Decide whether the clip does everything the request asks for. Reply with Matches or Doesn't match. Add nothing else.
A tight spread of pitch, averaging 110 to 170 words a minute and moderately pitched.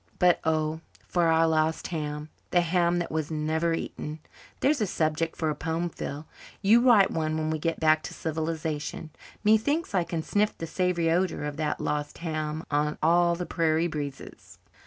Doesn't match